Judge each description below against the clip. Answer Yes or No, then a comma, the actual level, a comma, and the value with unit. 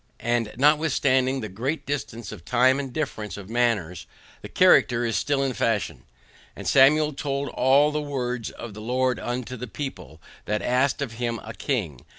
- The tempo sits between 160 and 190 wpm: Yes, average, 170 wpm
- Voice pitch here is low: Yes, low, 125 Hz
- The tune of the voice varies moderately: Yes, average, 3.5 semitones